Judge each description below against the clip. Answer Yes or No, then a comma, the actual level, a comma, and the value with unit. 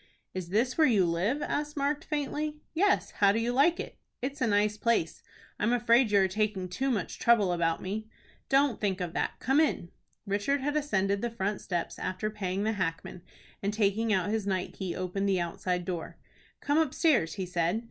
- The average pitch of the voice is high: Yes, high, 210 Hz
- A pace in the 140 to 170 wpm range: No, average, 200 wpm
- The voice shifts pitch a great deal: Yes, wide, 5.9 semitones